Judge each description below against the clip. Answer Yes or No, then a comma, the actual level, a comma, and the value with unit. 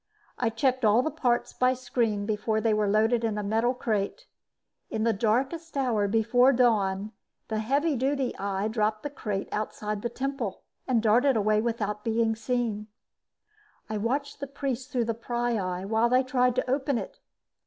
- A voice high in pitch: Yes, high, 230 Hz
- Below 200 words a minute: Yes, average, 170 wpm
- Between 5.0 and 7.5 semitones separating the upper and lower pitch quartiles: No, average, 3.1 semitones